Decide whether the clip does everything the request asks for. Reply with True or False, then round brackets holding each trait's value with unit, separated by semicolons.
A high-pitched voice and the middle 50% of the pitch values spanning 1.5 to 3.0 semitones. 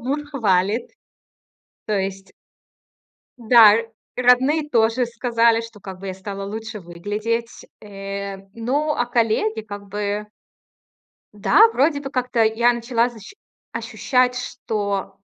False (225 Hz; 3.4 semitones)